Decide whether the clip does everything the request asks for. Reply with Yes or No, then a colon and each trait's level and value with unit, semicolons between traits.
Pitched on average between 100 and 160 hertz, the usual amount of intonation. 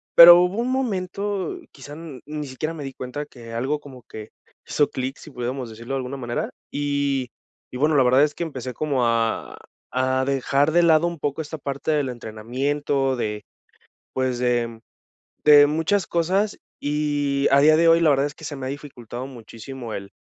Yes: medium, 140 Hz; average, 3.4 semitones